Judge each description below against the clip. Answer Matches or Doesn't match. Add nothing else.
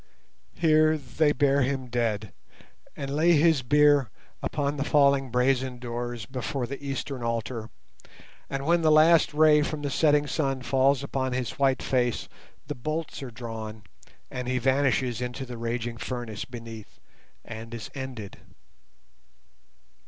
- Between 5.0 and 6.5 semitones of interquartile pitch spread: Doesn't match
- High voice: Doesn't match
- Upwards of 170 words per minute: Doesn't match